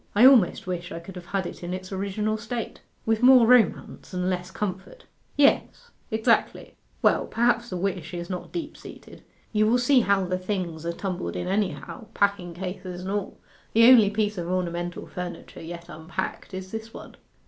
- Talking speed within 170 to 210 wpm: Yes, average, 180 wpm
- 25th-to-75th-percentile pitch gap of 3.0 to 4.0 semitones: Yes, average, 3.6 semitones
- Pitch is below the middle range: No, high, 190 Hz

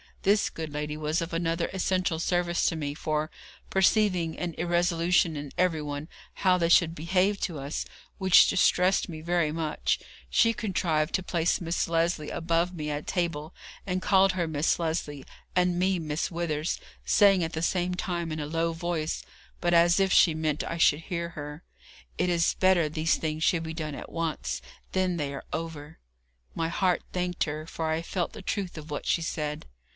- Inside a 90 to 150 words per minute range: No, average, 180 wpm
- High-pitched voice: No, medium, 165 Hz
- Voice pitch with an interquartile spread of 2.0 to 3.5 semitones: Yes, narrow, 2.4 semitones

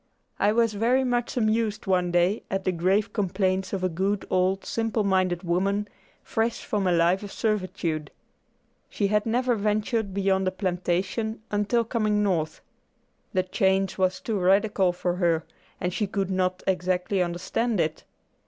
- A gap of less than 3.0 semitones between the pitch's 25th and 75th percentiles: Yes, narrow, 2.6 semitones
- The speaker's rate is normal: Yes, average, 155 wpm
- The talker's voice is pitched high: Yes, high, 195 Hz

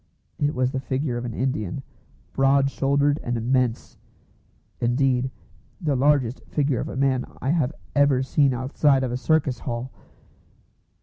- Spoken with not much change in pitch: Yes, narrow, 2.1 semitones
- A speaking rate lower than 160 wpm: Yes, average, 145 wpm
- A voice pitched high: No, low, 130 Hz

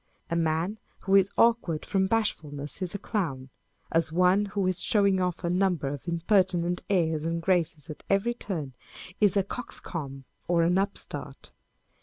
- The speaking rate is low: No, average, 165 wpm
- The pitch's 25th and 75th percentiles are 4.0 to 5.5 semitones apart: No, average, 3.4 semitones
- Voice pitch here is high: No, medium, 180 Hz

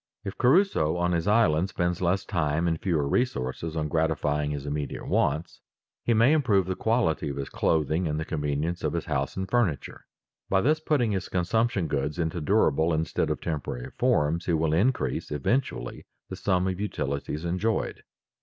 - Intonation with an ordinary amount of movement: Yes, average, 4.6 semitones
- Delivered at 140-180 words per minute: Yes, average, 175 wpm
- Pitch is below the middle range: Yes, very low, 85 Hz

